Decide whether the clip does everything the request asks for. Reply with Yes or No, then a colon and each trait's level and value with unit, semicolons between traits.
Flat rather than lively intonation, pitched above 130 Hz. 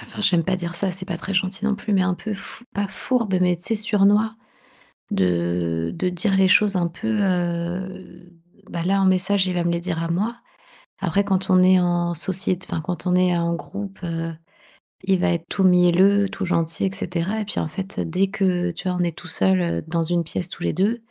Yes: narrow, 2.2 semitones; medium, 185 Hz